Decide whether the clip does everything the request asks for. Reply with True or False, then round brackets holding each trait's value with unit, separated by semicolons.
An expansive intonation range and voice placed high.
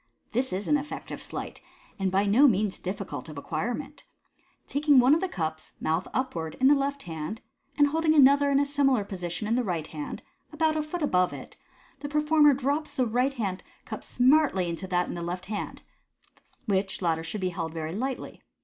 True (7.8 semitones; 230 Hz)